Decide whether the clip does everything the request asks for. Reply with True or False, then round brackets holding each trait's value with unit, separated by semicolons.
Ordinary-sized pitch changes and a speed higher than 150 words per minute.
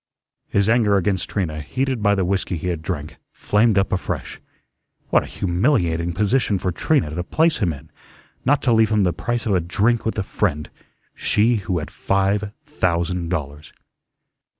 True (4.3 semitones; 175 wpm)